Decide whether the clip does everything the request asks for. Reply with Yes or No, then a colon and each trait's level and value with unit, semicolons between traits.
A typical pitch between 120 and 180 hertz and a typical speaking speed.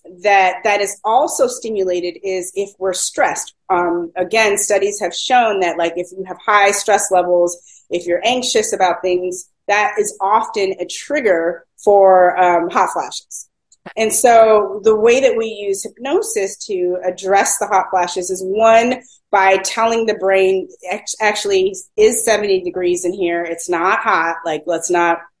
No: high, 195 Hz; average, 160 wpm